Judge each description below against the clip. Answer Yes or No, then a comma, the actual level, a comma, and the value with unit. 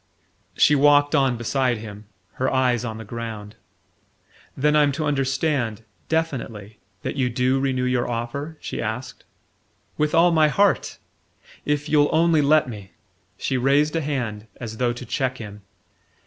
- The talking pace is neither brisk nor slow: Yes, average, 155 wpm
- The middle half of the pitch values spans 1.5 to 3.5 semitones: No, average, 4.3 semitones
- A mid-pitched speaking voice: No, low, 130 Hz